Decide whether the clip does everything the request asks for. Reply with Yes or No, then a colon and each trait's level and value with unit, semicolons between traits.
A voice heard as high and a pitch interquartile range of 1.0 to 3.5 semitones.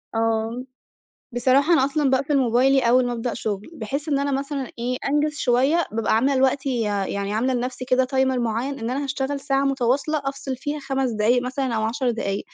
Yes: very high, 260 Hz; average, 2.8 semitones